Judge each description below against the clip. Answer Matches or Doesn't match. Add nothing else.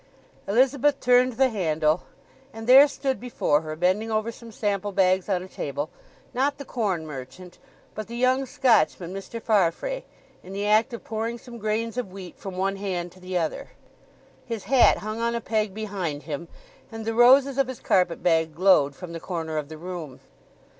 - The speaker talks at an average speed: Matches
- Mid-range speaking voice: Doesn't match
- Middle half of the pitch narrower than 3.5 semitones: Doesn't match